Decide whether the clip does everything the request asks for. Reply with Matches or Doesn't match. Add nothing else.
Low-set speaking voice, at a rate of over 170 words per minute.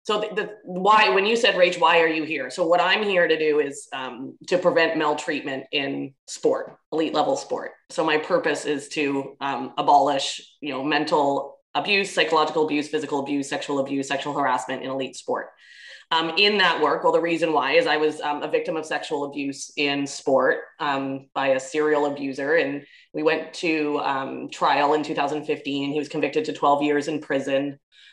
Doesn't match